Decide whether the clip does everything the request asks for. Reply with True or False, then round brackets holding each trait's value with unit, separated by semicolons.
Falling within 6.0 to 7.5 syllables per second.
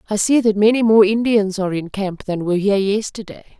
True (6.1 syllables/s)